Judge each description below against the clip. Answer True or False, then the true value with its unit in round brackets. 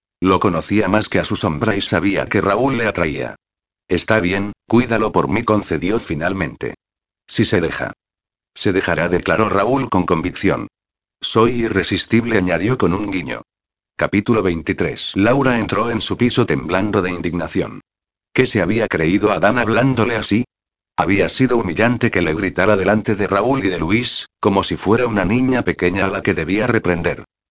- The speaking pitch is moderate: False (100 Hz)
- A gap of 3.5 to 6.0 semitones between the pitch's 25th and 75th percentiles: True (3.8 semitones)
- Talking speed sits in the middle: True (165 wpm)